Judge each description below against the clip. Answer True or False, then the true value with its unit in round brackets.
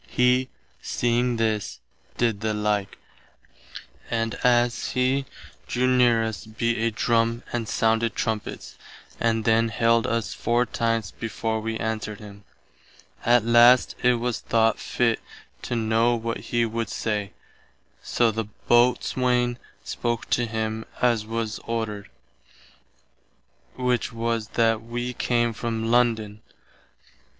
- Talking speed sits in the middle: False (125 wpm)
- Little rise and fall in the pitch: True (1.4 semitones)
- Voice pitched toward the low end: True (115 Hz)